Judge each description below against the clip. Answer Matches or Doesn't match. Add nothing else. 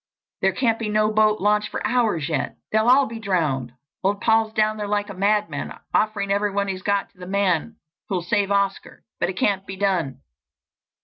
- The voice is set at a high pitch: Matches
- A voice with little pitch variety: Matches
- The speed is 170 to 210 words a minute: Matches